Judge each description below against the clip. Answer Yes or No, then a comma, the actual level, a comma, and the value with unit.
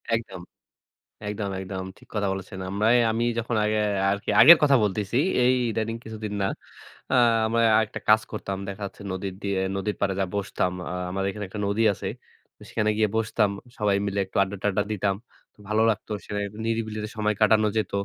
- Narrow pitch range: Yes, narrow, 2.0 semitones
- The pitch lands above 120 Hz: No, low, 105 Hz